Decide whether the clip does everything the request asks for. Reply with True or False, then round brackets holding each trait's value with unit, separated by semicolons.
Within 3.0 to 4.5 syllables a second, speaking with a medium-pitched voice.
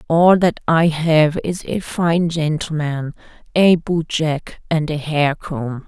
True (3.4 syllables/s; 160 Hz)